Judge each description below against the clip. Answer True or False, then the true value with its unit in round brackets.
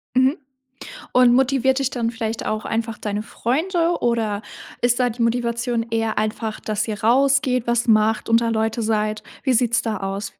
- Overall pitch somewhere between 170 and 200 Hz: False (230 Hz)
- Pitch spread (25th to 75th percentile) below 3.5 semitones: True (2.4 semitones)